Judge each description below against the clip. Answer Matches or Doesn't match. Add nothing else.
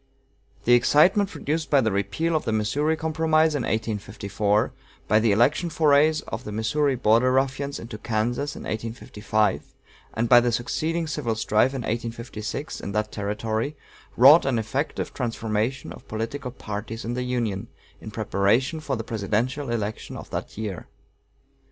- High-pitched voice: Doesn't match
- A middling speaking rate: Matches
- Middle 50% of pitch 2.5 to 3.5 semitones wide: Doesn't match